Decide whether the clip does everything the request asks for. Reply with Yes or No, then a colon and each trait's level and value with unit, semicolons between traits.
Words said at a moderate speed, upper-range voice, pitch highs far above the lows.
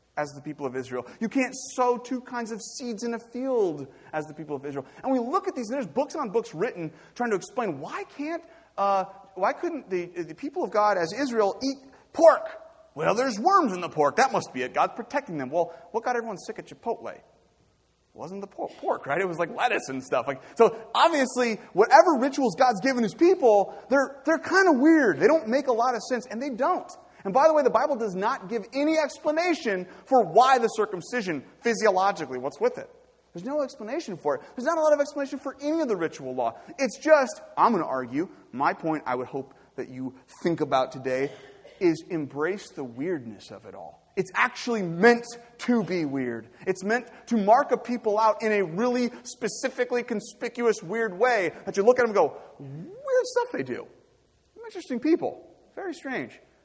No: fast, 210 wpm; high, 235 Hz; wide, 7.1 semitones